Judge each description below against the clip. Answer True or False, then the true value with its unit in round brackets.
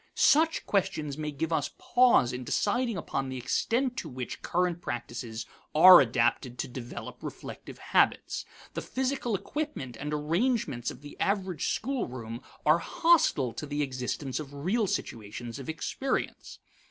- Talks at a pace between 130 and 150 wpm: True (140 wpm)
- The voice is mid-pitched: True (150 Hz)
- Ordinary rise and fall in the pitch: False (8.8 semitones)